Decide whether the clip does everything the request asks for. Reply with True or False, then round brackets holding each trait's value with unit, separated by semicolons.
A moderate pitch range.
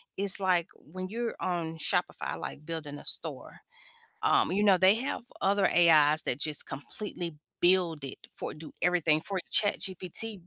True (3.9 semitones)